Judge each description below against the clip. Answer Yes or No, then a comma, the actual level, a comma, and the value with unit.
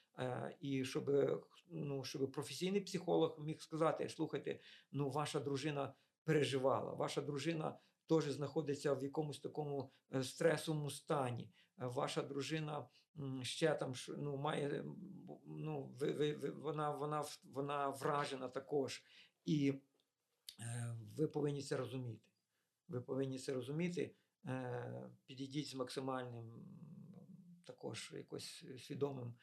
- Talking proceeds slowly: Yes, slow, 100 wpm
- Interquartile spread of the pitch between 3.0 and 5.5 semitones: No, narrow, 2.6 semitones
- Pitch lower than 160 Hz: Yes, medium, 140 Hz